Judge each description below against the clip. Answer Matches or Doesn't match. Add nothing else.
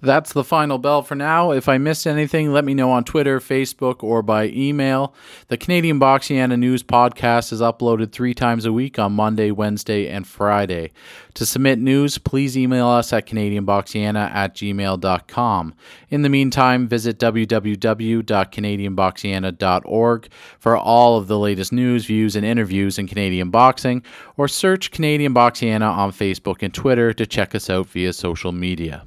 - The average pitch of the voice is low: Matches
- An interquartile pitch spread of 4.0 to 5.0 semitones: Matches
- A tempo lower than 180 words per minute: Matches